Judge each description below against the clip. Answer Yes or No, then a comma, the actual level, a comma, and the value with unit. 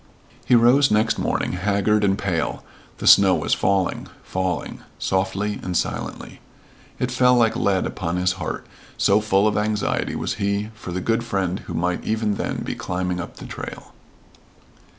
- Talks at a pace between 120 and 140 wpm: No, average, 165 wpm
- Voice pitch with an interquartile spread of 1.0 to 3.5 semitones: Yes, average, 2.7 semitones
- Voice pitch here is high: No, low, 100 Hz